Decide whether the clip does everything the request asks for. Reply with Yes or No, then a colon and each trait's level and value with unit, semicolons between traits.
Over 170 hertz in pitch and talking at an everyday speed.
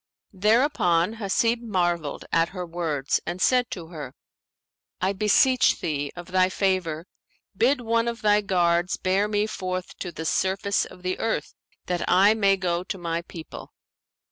Yes: medium, 185 Hz; average, 155 wpm